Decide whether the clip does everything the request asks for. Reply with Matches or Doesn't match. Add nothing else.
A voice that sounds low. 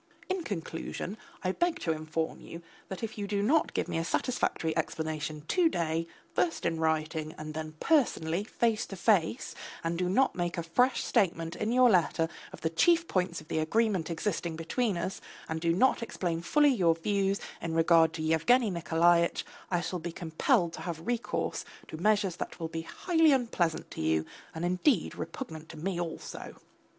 Doesn't match